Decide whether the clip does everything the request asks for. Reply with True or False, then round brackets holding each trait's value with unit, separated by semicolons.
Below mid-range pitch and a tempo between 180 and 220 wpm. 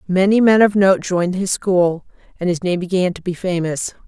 False (185 Hz; 205 wpm)